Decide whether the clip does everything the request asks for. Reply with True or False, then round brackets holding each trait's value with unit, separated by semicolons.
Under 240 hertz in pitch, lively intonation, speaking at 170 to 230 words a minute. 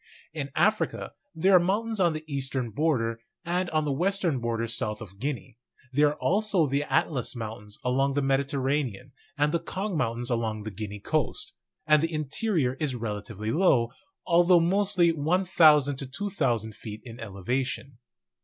False (140 Hz; 6.5 semitones; 155 wpm)